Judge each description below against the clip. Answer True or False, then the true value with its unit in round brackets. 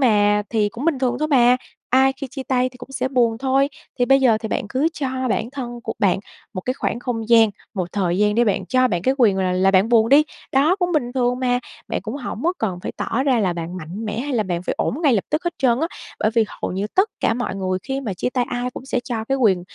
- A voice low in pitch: False (245 Hz)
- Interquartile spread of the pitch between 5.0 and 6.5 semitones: False (4.2 semitones)